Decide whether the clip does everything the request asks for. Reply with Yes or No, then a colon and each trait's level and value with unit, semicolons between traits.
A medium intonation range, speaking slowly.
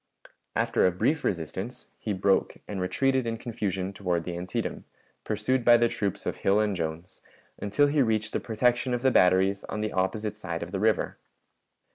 No: average, 4.2 semitones; average, 180 wpm